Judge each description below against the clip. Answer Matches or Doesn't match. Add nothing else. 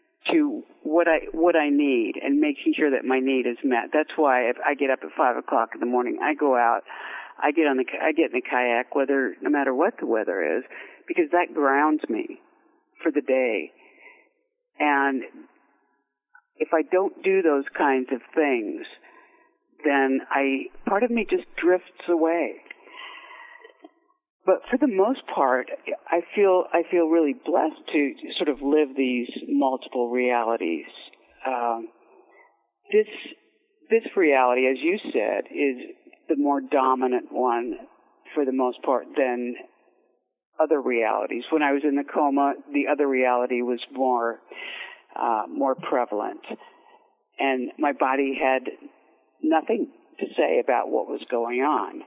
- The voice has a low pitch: Doesn't match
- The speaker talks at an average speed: Matches